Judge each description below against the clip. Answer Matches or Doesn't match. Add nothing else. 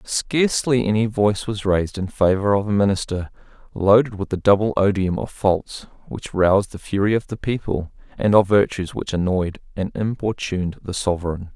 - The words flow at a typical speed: Matches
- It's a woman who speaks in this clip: Doesn't match